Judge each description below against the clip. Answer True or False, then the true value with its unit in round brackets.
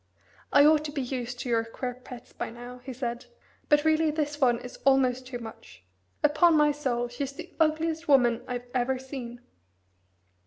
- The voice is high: True (260 Hz)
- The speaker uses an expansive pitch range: False (3.4 semitones)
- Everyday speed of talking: True (180 wpm)